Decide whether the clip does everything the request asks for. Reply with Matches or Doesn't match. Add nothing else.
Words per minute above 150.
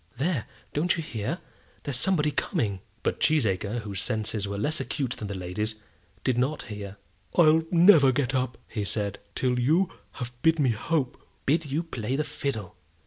Matches